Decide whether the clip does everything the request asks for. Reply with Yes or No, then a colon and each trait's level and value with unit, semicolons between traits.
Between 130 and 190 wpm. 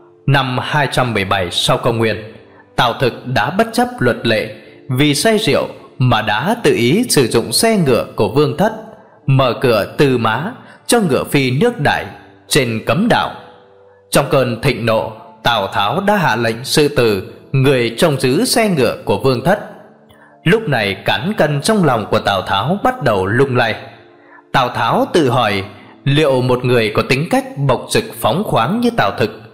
Yes: average, 175 wpm